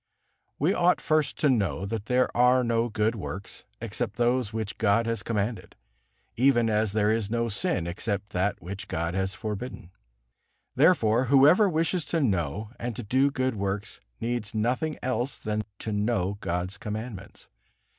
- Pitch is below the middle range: Yes, low, 110 Hz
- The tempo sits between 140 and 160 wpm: Yes, average, 155 wpm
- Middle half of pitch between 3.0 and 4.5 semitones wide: Yes, average, 3.9 semitones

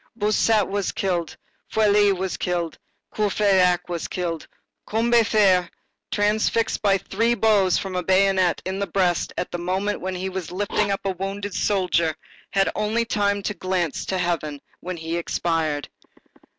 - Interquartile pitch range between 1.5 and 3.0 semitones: Yes, narrow, 2.5 semitones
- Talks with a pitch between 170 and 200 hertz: Yes, high, 190 Hz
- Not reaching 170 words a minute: Yes, average, 155 wpm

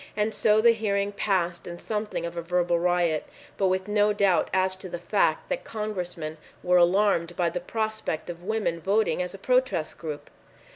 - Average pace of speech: Yes, average, 185 wpm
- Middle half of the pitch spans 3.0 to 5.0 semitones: Yes, average, 3.4 semitones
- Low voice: No, medium, 185 Hz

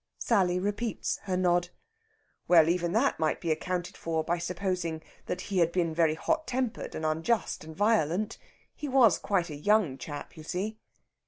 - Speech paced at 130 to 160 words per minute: No, average, 170 wpm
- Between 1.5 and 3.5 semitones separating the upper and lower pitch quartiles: No, average, 4.3 semitones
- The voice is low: No, medium, 180 Hz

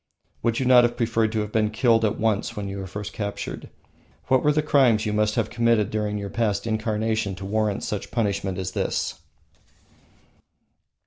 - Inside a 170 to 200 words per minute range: Yes, average, 185 wpm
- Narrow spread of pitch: Yes, narrow, 2.0 semitones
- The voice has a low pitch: Yes, low, 110 Hz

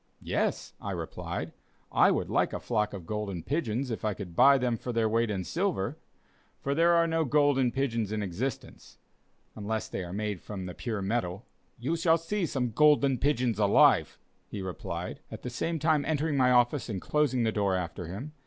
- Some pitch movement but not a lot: No, wide, 5.7 semitones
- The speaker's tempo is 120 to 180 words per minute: No, average, 190 wpm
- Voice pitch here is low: Yes, low, 120 Hz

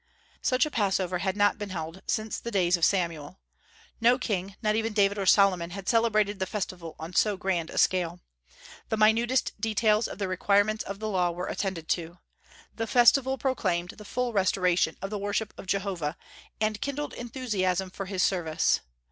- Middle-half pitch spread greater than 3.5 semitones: No, average, 3.2 semitones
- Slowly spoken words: No, average, 180 wpm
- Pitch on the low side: No, high, 200 Hz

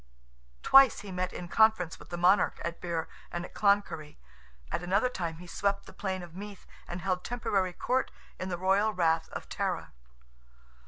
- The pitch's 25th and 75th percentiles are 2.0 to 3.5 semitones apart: Yes, average, 2.8 semitones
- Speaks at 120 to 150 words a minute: No, average, 170 wpm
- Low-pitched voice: No, medium, 185 Hz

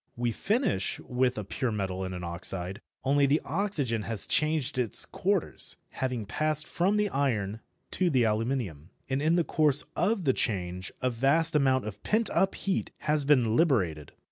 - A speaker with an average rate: Yes, average, 170 wpm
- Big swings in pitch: Yes, wide, 6.5 semitones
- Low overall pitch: Yes, low, 130 Hz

